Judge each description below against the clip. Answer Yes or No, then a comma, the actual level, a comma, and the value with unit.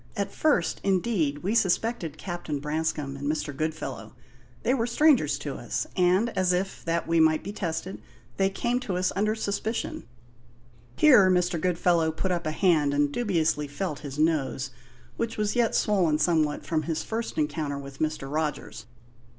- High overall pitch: No, medium, 170 Hz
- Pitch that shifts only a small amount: No, average, 4.6 semitones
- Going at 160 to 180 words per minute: Yes, average, 165 wpm